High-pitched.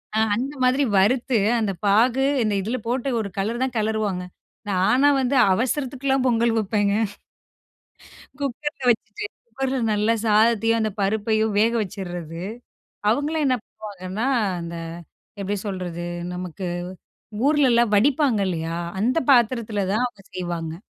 Yes: high, 220 Hz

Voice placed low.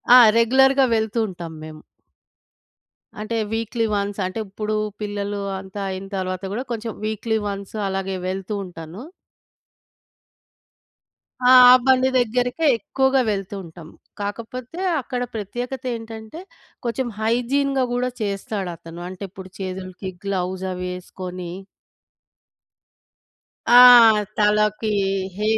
No: high, 210 Hz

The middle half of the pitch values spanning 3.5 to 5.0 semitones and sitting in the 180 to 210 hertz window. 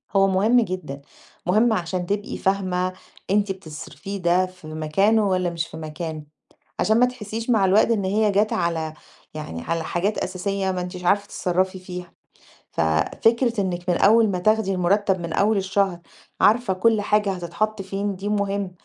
No: average, 2.7 semitones; high, 190 Hz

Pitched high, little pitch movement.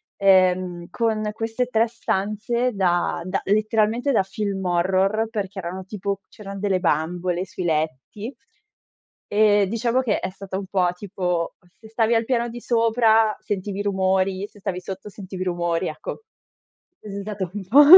No: high, 200 Hz; average, 3.0 semitones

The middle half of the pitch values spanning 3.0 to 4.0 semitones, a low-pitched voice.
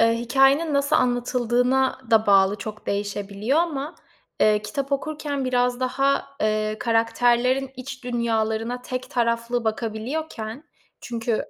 No: average, 3.4 semitones; high, 245 Hz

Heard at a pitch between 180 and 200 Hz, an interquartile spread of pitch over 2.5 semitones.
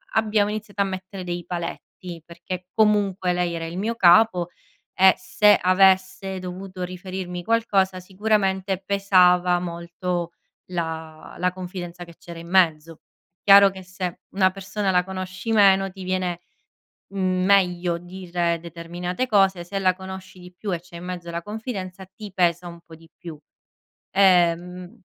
No: medium, 185 Hz; narrow, 1.7 semitones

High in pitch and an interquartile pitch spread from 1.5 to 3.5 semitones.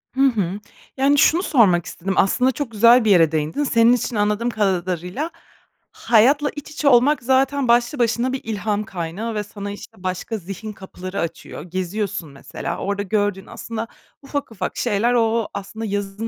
No: high, 215 Hz; average, 4.0 semitones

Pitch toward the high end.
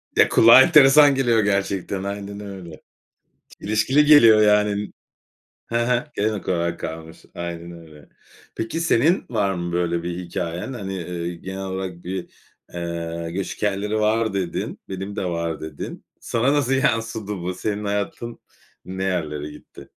No: low, 100 Hz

